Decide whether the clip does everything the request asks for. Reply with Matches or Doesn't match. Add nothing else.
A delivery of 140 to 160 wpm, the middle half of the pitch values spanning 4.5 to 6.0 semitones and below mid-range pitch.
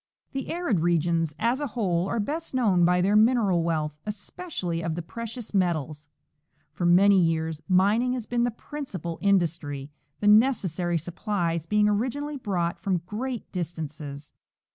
Doesn't match